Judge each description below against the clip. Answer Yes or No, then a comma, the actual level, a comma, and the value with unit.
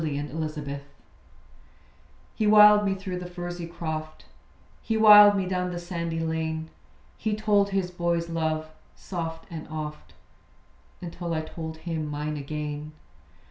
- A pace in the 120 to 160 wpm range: Yes, average, 140 wpm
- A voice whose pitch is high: No, medium, 165 Hz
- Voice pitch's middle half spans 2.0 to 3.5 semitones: Yes, average, 2.7 semitones